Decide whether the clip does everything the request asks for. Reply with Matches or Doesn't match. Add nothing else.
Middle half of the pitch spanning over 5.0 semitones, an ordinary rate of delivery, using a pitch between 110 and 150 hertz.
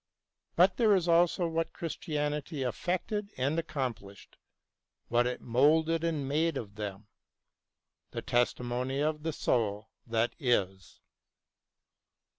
Doesn't match